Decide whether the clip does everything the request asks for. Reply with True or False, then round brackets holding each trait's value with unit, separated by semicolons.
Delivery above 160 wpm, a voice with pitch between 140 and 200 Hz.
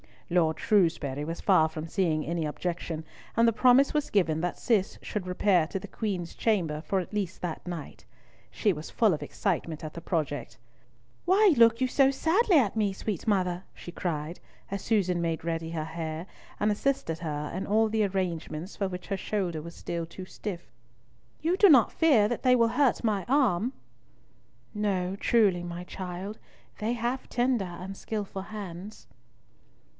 True (170 wpm; 190 Hz)